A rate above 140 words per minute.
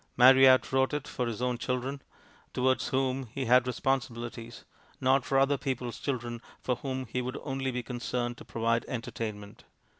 Yes: average, 160 wpm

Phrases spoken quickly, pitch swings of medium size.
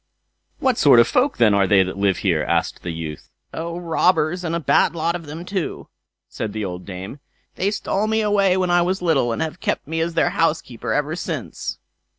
No: fast, 210 wpm; wide, 8.8 semitones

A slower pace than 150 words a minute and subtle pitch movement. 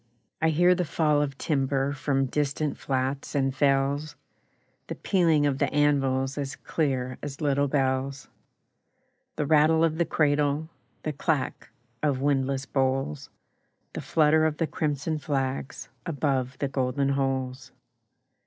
Yes: slow, 135 wpm; narrow, 2.1 semitones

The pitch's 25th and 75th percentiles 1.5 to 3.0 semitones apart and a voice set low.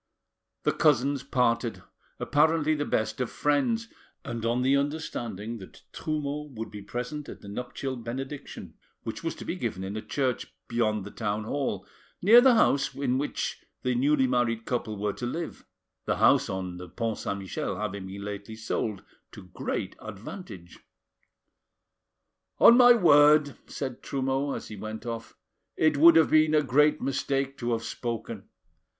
No: average, 5.2 semitones; low, 125 Hz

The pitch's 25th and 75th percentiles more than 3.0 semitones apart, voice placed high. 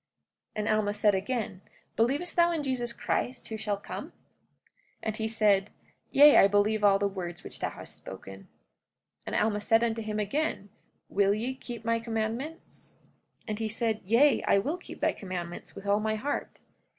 No: average, 2.7 semitones; high, 215 Hz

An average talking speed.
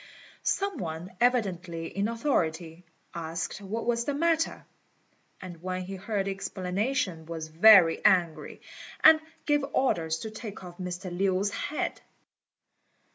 No: slow, 130 wpm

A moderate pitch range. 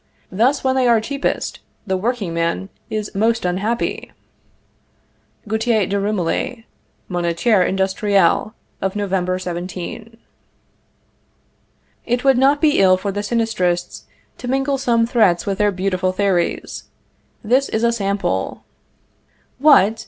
Yes: average, 4.1 semitones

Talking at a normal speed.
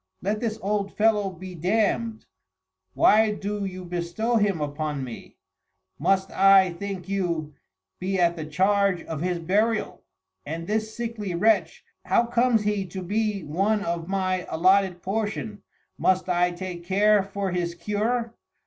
Yes: average, 145 wpm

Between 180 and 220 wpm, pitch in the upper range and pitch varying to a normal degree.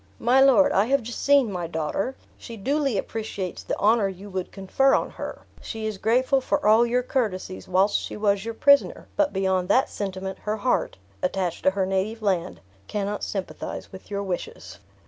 Yes: average, 185 wpm; high, 210 Hz; average, 4.3 semitones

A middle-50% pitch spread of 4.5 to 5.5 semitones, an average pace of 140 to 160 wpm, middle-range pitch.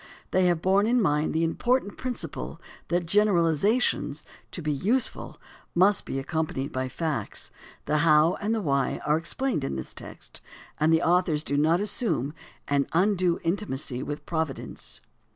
Yes: average, 5.1 semitones; average, 155 wpm; medium, 165 Hz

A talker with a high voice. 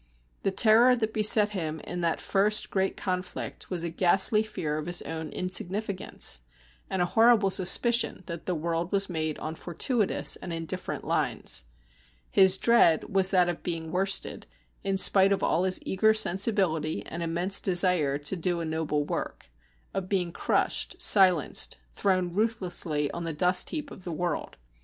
No: medium, 180 Hz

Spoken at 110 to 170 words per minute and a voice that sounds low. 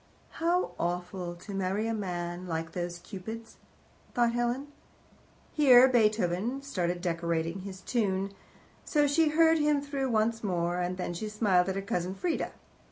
No: average, 150 wpm; high, 195 Hz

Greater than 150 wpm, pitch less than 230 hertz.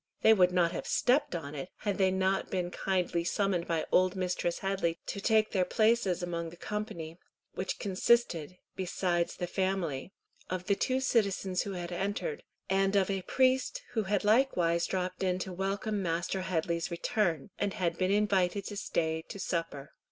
Yes: average, 175 wpm; medium, 185 Hz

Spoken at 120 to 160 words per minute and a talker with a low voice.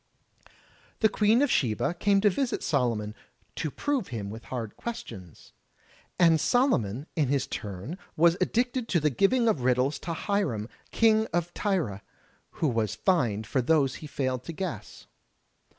No: average, 150 wpm; medium, 155 Hz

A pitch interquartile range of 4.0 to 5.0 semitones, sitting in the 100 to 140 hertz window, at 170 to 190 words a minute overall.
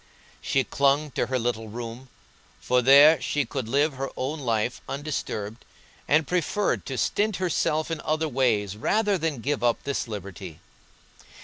No: average, 4.4 semitones; low, 135 Hz; average, 150 wpm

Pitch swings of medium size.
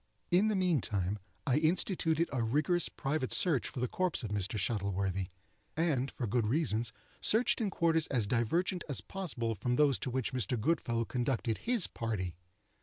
No: wide, 7.0 semitones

